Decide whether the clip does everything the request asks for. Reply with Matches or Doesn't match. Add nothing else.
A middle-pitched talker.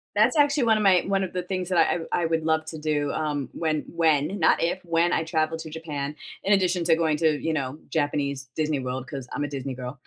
Matches